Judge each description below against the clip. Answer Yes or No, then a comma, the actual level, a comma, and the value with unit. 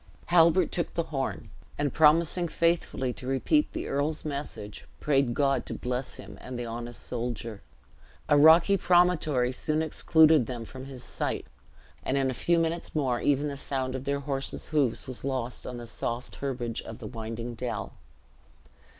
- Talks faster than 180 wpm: No, average, 165 wpm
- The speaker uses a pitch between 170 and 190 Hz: No, low, 135 Hz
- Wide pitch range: No, average, 4.2 semitones